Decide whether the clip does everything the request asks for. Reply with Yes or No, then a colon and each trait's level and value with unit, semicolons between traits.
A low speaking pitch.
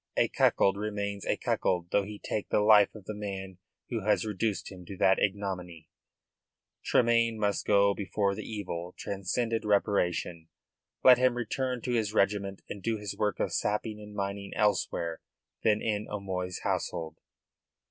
Yes: low, 100 Hz